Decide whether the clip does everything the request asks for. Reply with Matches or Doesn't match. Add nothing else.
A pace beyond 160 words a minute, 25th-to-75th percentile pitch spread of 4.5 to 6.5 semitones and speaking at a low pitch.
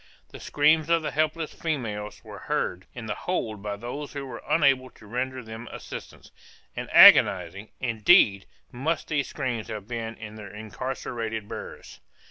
Doesn't match